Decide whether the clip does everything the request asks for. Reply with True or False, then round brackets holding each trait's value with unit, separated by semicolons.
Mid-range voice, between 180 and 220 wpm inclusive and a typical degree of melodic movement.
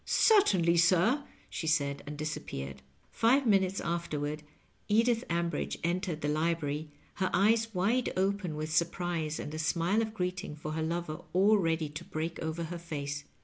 False (170 Hz; 165 wpm; 4.0 semitones)